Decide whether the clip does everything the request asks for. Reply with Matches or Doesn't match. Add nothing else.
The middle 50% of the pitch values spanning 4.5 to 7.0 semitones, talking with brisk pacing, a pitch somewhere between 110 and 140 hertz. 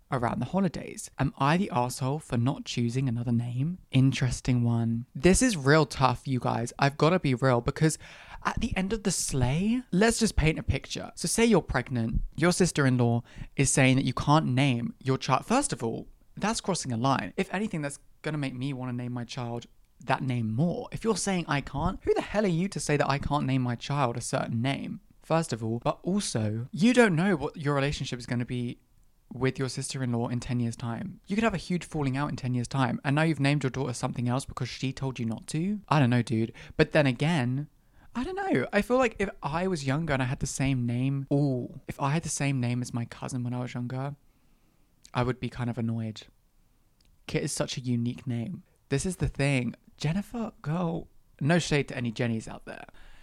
Matches